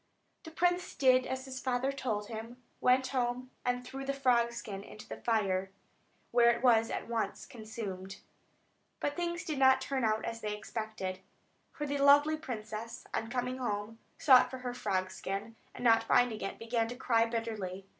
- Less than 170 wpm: No, average, 175 wpm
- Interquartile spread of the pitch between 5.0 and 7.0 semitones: No, average, 3.1 semitones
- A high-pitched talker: Yes, high, 235 Hz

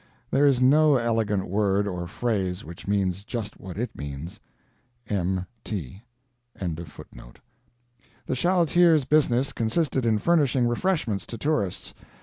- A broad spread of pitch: Yes, wide, 5.7 semitones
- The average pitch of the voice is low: Yes, low, 115 Hz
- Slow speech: Yes, slow, 115 wpm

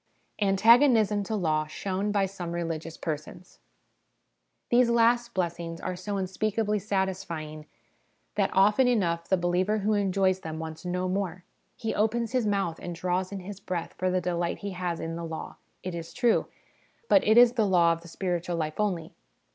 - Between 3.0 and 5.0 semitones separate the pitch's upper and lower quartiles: Yes, average, 3.5 semitones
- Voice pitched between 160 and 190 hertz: Yes, medium, 185 Hz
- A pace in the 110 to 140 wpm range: No, average, 170 wpm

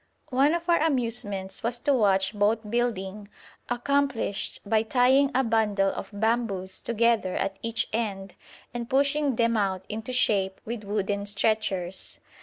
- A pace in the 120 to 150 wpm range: Yes, average, 140 wpm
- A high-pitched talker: Yes, high, 220 Hz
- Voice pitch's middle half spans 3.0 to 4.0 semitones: Yes, average, 3.5 semitones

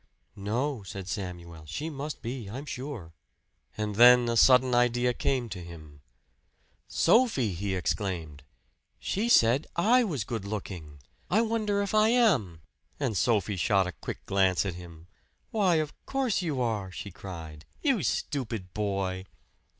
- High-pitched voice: No, low, 110 Hz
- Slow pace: No, average, 145 wpm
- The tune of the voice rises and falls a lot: Yes, wide, 7.9 semitones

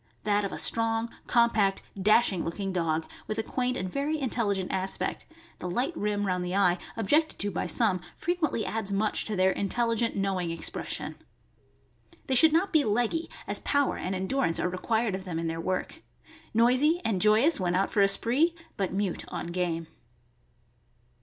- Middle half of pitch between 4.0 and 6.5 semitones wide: Yes, average, 4.5 semitones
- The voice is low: No, high, 205 Hz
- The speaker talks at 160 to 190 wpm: Yes, average, 185 wpm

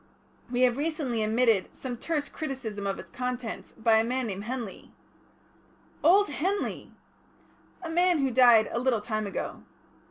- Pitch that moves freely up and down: No, average, 4.4 semitones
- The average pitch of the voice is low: No, very high, 250 Hz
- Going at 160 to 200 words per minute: No, average, 150 wpm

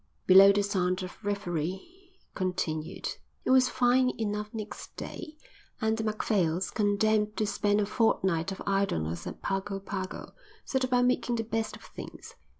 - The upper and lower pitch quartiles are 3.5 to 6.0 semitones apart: No, average, 3.0 semitones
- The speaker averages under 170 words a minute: Yes, average, 150 wpm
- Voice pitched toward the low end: No, high, 205 Hz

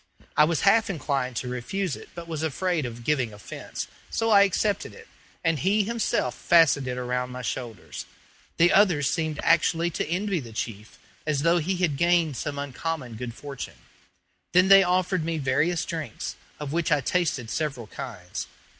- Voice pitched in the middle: Yes, medium, 155 Hz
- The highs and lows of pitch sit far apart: Yes, wide, 5.7 semitones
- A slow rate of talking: No, average, 170 wpm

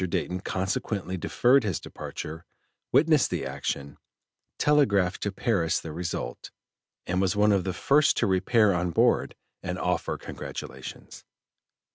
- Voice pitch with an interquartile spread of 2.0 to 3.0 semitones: No, average, 3.5 semitones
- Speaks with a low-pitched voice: Yes, very low, 95 Hz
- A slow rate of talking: Yes, slow, 130 wpm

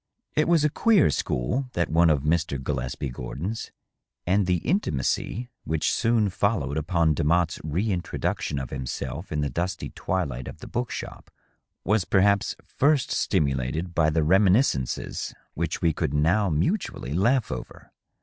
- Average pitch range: No, wide, 6.1 semitones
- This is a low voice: Yes, very low, 85 Hz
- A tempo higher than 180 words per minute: No, average, 150 wpm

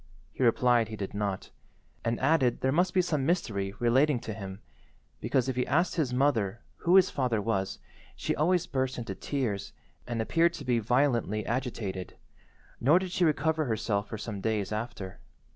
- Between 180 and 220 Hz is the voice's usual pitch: No, low, 120 Hz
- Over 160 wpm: Yes, average, 175 wpm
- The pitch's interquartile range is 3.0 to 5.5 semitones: Yes, average, 5.2 semitones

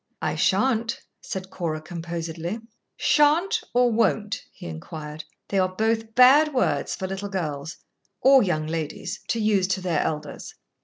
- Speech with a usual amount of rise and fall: No, wide, 6.1 semitones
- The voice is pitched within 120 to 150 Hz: No, high, 190 Hz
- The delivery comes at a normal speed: Yes, average, 145 wpm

